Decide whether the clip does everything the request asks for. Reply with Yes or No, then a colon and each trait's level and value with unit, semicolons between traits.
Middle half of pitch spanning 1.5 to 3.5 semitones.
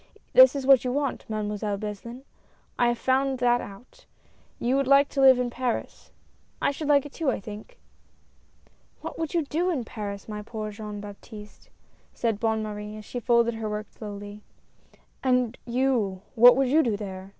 No: average, 4.0 semitones